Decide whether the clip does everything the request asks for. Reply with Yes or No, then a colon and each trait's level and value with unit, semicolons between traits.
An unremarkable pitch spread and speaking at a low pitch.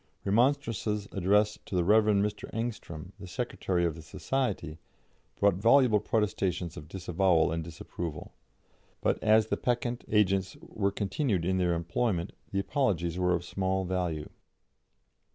Yes: average, 3.5 semitones; very low, 95 Hz